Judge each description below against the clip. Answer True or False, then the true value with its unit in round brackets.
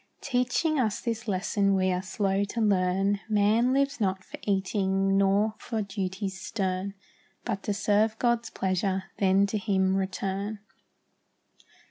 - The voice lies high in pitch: True (200 Hz)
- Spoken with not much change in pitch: True (2.2 semitones)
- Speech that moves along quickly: False (135 wpm)